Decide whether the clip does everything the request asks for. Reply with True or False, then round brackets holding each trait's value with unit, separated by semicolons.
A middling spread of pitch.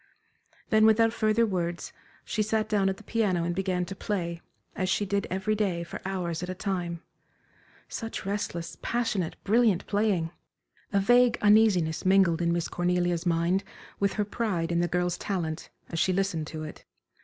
True (3.5 semitones)